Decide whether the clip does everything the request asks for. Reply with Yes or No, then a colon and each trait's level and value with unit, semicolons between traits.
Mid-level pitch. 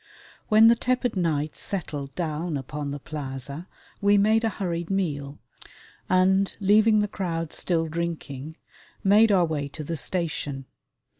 Yes: medium, 170 Hz